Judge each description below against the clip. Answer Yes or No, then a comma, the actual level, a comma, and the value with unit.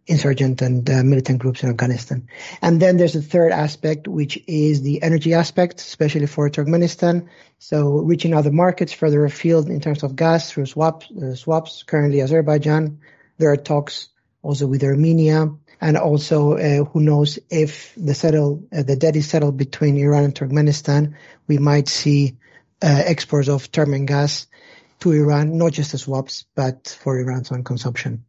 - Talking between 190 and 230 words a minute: No, average, 170 wpm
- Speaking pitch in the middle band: Yes, medium, 150 Hz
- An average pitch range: No, narrow, 2.3 semitones